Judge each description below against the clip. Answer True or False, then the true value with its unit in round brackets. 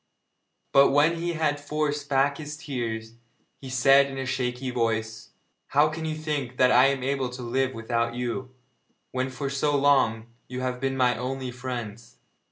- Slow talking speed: False (175 wpm)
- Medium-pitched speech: False (130 Hz)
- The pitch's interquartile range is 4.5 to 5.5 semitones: False (2.5 semitones)